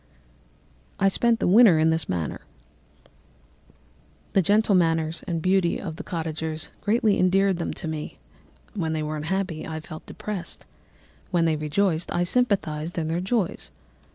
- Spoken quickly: No, average, 155 wpm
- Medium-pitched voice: Yes, medium, 170 Hz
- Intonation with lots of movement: No, average, 3.6 semitones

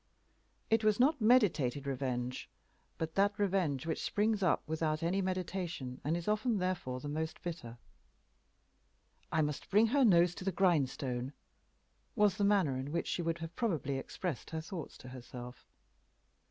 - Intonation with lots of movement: Yes, wide, 6.0 semitones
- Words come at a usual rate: Yes, average, 155 wpm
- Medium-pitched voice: Yes, medium, 165 Hz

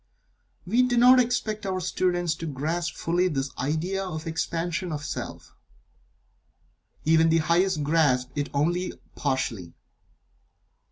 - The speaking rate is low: Yes, slow, 125 wpm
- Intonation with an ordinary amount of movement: Yes, average, 3.7 semitones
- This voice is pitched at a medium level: Yes, medium, 165 Hz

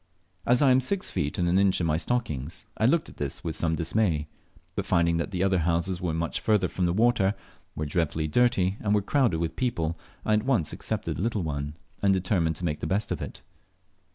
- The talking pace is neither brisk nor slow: No, fast, 220 wpm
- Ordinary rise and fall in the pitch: Yes, average, 4.9 semitones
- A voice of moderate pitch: No, very low, 90 Hz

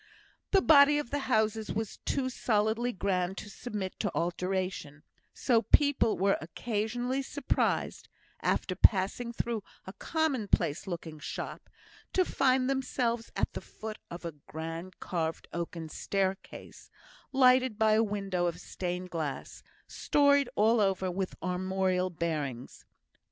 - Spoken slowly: Yes, slow, 130 wpm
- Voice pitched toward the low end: No, high, 205 Hz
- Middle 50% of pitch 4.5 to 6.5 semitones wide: Yes, average, 5.3 semitones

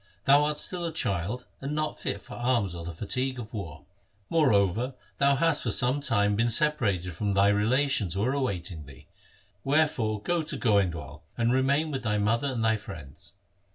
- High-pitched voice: No, low, 115 Hz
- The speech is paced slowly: No, average, 185 wpm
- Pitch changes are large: Yes, wide, 5.8 semitones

